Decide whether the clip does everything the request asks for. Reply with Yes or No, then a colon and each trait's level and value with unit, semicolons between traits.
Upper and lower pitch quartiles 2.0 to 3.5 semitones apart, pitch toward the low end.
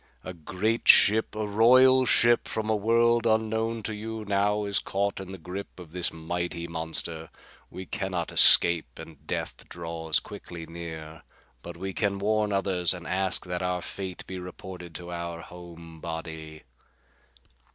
No: average, 3.9 semitones; very low, 90 Hz